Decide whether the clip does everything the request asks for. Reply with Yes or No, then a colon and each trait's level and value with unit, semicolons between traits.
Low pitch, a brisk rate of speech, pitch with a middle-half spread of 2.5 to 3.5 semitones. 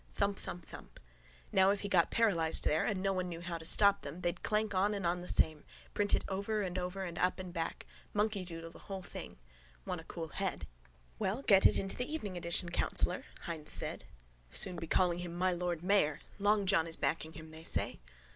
No: medium, 180 Hz; fast, 215 wpm; average, 3.0 semitones